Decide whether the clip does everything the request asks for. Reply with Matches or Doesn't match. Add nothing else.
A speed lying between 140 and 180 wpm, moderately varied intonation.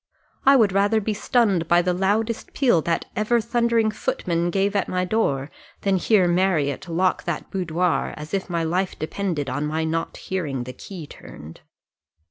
Matches